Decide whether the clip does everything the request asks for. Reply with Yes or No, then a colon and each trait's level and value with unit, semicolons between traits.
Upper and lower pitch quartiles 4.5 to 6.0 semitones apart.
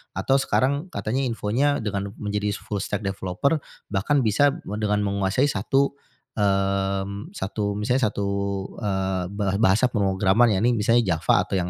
No: average, 3.7 semitones